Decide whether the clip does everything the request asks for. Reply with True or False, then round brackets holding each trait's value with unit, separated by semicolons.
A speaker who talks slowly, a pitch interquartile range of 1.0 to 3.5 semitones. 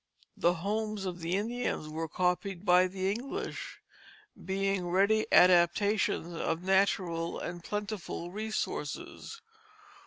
True (105 wpm; 3.0 semitones)